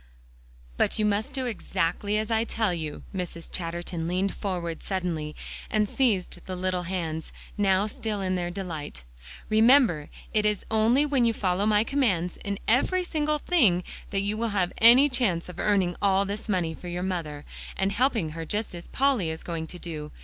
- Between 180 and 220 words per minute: Yes, average, 185 wpm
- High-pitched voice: Yes, high, 195 Hz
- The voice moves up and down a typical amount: Yes, average, 4.1 semitones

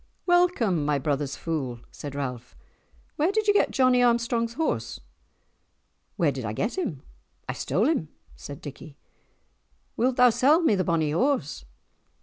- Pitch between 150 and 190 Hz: Yes, medium, 185 Hz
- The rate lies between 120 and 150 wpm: Yes, average, 145 wpm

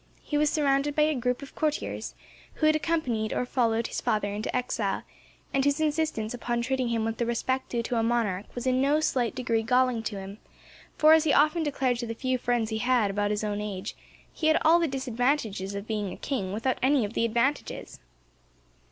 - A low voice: No, high, 245 Hz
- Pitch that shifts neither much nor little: Yes, average, 4.2 semitones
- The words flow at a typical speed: No, fast, 215 wpm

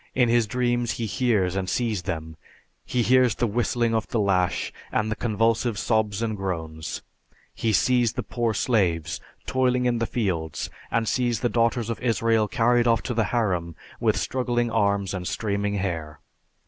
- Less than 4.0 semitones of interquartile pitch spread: Yes, average, 3.6 semitones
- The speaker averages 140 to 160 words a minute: No, average, 170 wpm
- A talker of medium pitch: No, low, 115 Hz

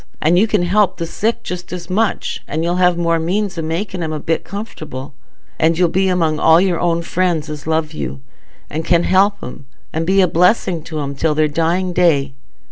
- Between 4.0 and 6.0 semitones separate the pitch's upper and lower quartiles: No, narrow, 2.6 semitones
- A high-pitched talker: No, medium, 170 Hz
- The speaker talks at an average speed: No, fast, 210 wpm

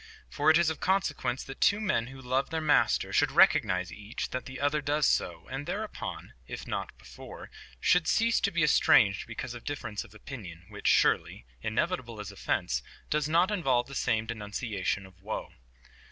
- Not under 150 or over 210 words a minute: Yes, average, 180 wpm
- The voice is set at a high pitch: No, low, 130 Hz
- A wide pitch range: Yes, wide, 6.4 semitones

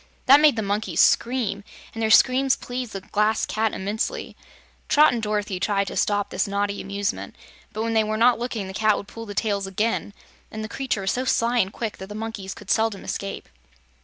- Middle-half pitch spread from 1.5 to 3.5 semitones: Yes, narrow, 2.4 semitones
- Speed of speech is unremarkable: No, fast, 210 wpm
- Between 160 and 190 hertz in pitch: No, high, 215 Hz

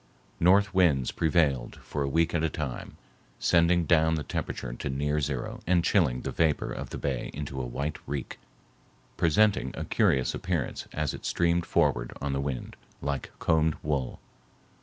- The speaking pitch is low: Yes, very low, 75 Hz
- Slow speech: No, average, 160 wpm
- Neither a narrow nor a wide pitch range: Yes, average, 3.7 semitones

